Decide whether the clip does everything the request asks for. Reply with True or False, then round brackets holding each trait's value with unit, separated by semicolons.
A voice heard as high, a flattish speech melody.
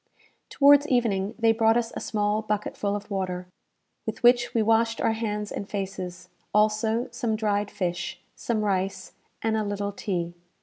True (210 Hz; 2.1 semitones)